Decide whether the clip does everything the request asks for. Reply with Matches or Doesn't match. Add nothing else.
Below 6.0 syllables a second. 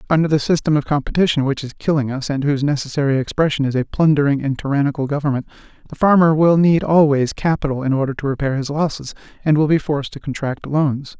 Doesn't match